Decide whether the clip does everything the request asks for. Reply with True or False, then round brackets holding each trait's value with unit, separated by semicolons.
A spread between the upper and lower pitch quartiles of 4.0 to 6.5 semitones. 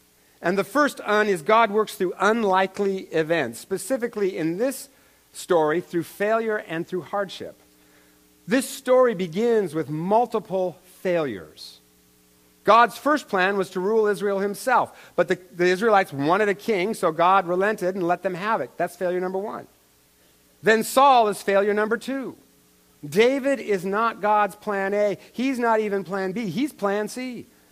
True (4.4 semitones)